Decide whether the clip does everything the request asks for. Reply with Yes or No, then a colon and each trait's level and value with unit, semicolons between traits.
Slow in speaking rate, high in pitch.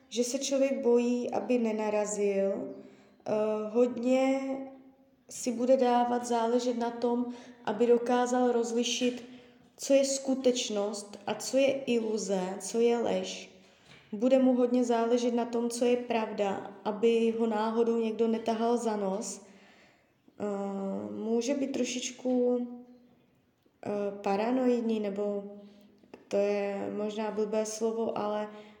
Yes: slow, 110 wpm; high, 235 Hz